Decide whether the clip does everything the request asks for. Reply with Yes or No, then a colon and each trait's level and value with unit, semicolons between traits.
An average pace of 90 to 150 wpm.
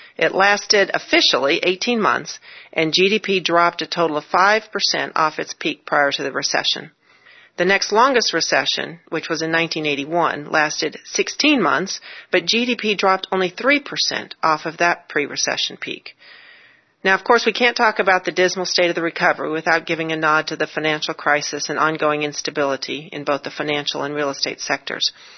No: average, 175 wpm